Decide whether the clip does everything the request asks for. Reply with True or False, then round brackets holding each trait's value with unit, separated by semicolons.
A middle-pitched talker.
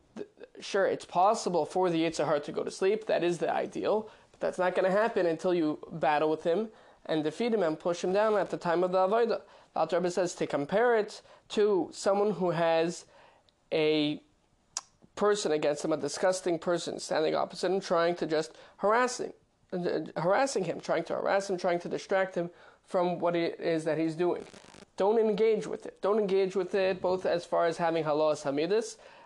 True (180 Hz)